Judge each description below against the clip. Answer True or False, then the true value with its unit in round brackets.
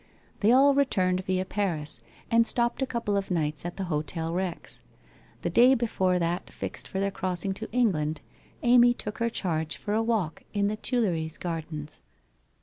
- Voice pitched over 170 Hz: True (190 Hz)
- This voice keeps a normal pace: True (170 wpm)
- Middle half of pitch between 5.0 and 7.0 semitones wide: True (5.6 semitones)